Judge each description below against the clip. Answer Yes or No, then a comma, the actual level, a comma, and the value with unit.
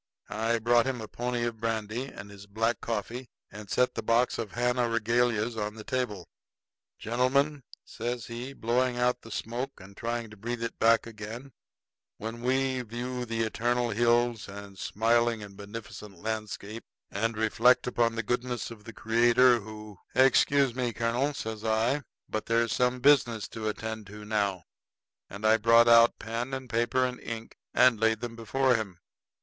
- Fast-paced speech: No, average, 170 wpm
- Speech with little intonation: Yes, narrow, 2.1 semitones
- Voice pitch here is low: Yes, low, 115 Hz